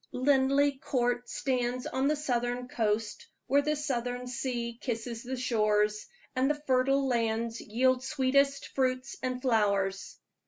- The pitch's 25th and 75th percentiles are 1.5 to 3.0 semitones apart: Yes, narrow, 2.4 semitones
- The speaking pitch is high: Yes, very high, 250 Hz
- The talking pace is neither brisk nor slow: No, slow, 130 wpm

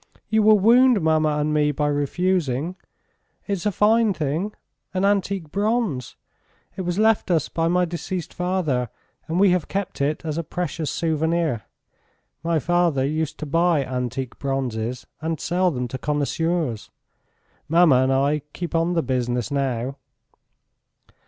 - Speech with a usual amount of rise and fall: Yes, average, 4.4 semitones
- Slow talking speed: No, average, 145 wpm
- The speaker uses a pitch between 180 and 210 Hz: No, medium, 160 Hz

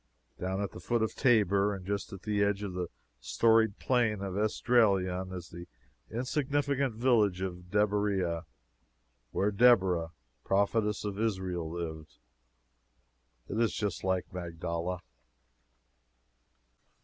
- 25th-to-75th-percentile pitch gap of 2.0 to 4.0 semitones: Yes, average, 3.4 semitones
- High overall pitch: No, low, 100 Hz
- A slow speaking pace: Yes, slow, 120 wpm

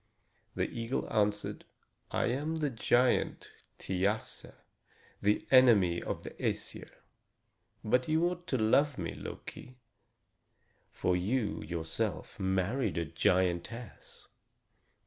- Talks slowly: Yes, slow, 105 wpm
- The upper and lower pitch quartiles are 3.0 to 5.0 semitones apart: No, wide, 5.6 semitones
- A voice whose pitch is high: No, low, 110 Hz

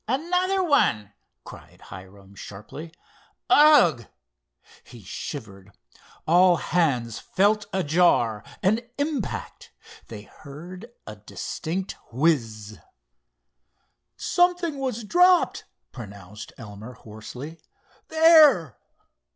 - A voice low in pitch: No, medium, 160 Hz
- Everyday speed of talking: No, slow, 80 wpm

